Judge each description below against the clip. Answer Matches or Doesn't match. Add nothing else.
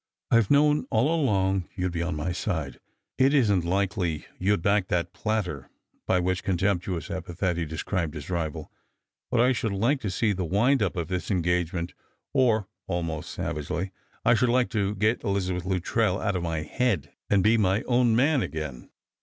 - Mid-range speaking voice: Doesn't match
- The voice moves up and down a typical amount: Matches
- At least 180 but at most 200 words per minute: Matches